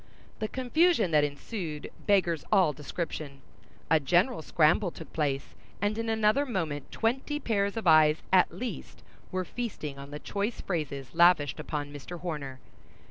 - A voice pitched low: No, medium, 170 Hz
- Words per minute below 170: Yes, average, 145 wpm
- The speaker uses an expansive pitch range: Yes, wide, 6.3 semitones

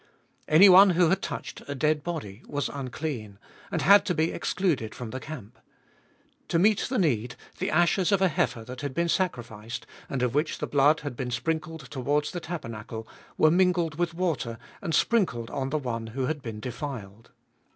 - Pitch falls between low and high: Yes, medium, 145 Hz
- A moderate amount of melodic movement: No, wide, 6.0 semitones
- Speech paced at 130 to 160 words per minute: No, average, 180 wpm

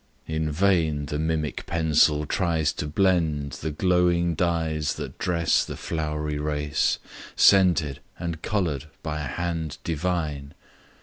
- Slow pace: Yes, slow, 125 wpm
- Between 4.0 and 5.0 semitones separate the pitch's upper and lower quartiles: No, narrow, 2.5 semitones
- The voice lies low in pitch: Yes, very low, 80 Hz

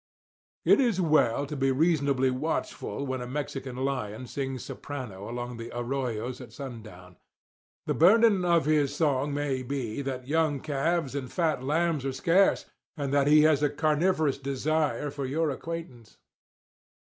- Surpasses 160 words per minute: No, average, 150 wpm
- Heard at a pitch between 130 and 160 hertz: Yes, medium, 140 Hz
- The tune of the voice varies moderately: Yes, average, 3.3 semitones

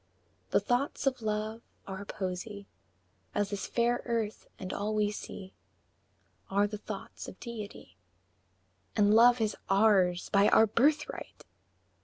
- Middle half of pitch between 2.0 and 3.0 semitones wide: Yes, narrow, 2.6 semitones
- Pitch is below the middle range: No, high, 210 Hz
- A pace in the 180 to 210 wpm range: No, slow, 135 wpm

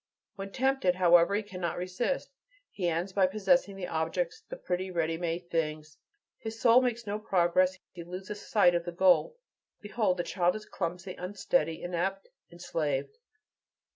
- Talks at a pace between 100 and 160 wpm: Yes, average, 150 wpm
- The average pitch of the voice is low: No, medium, 185 Hz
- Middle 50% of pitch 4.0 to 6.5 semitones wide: No, average, 3.2 semitones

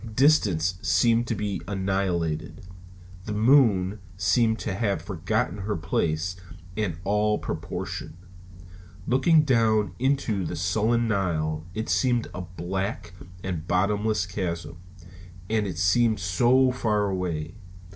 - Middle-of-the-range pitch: No, low, 100 Hz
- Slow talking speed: Yes, slow, 115 wpm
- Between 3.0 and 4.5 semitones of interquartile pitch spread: Yes, average, 3.9 semitones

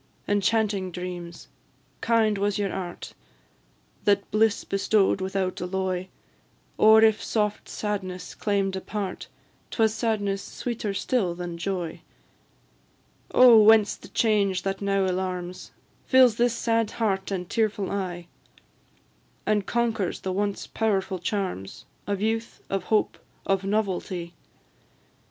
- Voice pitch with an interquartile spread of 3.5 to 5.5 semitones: No, average, 2.7 semitones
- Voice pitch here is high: Yes, high, 200 Hz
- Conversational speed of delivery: No, slow, 120 wpm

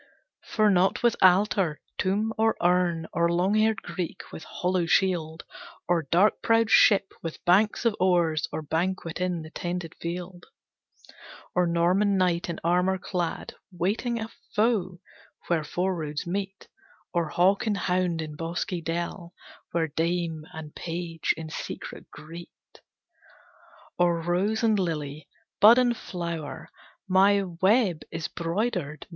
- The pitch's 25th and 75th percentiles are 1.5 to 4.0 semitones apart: Yes, average, 2.8 semitones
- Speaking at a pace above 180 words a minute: No, slow, 135 wpm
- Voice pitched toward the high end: No, medium, 175 Hz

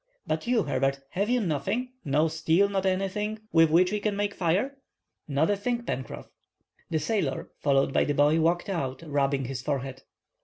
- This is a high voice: No, medium, 165 Hz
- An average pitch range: No, wide, 6.4 semitones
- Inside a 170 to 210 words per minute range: Yes, average, 180 wpm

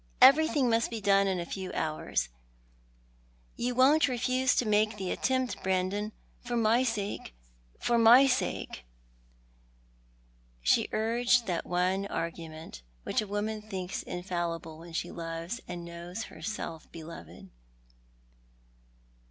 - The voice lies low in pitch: No, high, 200 Hz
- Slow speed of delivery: Yes, slow, 120 wpm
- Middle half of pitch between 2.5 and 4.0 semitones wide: No, wide, 5.6 semitones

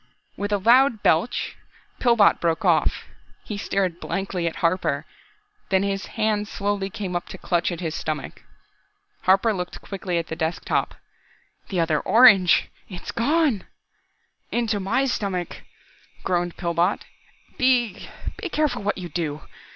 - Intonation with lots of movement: No, average, 3.9 semitones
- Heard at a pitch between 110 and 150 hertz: No, high, 195 Hz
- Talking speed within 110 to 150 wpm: Yes, average, 145 wpm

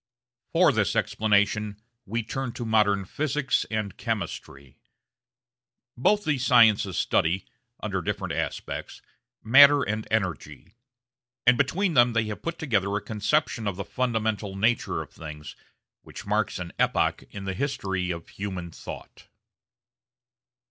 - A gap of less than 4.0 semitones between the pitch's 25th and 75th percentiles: No, average, 4.3 semitones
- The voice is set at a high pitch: No, low, 110 Hz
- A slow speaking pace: Yes, slow, 130 wpm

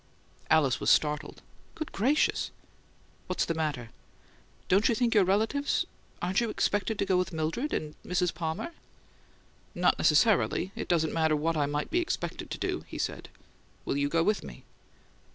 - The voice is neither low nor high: Yes, medium, 175 Hz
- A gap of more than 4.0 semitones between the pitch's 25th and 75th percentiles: Yes, wide, 5.4 semitones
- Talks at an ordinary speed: Yes, average, 165 wpm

